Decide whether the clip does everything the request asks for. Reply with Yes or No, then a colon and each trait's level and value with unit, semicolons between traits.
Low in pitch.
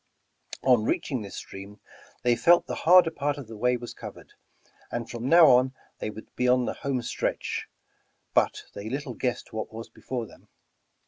Yes: low, 125 Hz